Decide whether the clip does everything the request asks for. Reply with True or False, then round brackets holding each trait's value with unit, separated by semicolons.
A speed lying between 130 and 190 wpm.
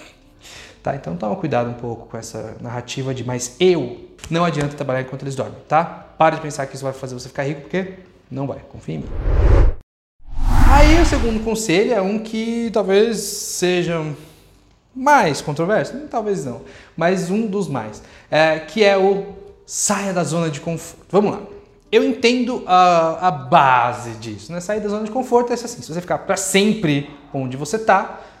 True (180 wpm)